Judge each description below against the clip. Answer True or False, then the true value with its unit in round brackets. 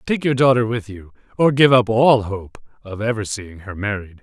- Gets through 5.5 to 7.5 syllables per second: False (4.9 syllables/s)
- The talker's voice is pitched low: True (115 Hz)